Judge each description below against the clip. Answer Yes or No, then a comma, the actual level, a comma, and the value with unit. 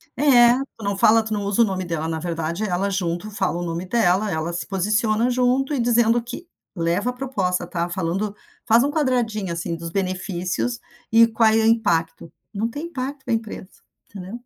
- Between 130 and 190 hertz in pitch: No, high, 205 Hz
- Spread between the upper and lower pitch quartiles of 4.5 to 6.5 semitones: Yes, average, 5.1 semitones